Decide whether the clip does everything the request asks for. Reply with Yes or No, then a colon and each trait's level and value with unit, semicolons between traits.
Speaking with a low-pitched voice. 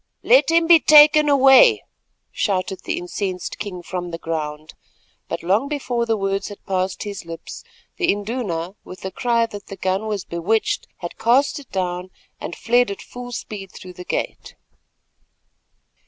No: high, 200 Hz